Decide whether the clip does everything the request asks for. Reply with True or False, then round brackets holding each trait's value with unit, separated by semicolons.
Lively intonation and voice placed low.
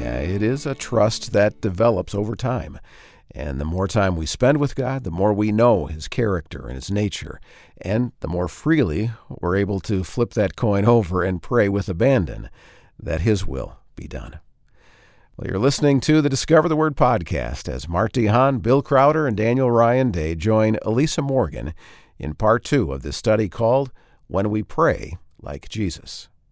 True (6.0 semitones; 105 Hz)